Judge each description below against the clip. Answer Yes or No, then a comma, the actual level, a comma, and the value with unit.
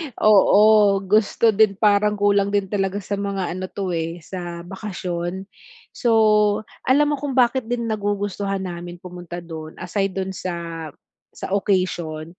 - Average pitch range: Yes, average, 3.0 semitones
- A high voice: Yes, high, 195 Hz